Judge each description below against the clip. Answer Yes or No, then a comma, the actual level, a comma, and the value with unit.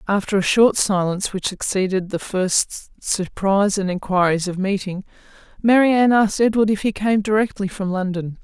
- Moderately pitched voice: No, high, 200 Hz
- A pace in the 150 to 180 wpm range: Yes, average, 155 wpm